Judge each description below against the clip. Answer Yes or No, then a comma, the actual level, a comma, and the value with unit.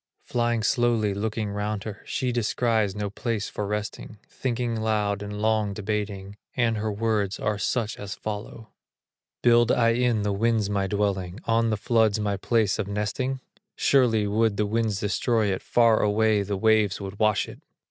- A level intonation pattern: Yes, narrow, 1.9 semitones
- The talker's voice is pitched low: Yes, low, 105 Hz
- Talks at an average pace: Yes, average, 170 wpm